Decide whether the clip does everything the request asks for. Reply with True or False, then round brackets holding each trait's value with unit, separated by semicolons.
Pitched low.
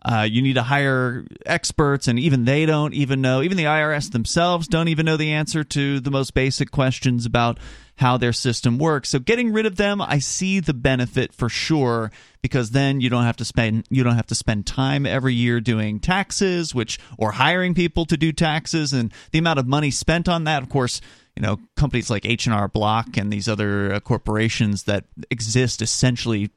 True (130 Hz)